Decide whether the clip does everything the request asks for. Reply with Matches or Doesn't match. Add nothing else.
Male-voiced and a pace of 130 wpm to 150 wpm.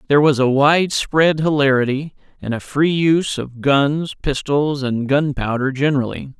Matches